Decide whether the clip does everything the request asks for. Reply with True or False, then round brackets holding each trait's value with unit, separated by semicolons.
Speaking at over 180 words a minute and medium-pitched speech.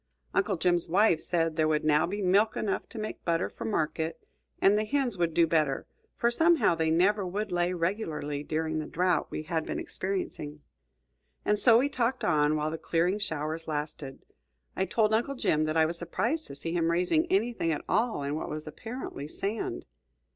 True (190 wpm; 175 Hz)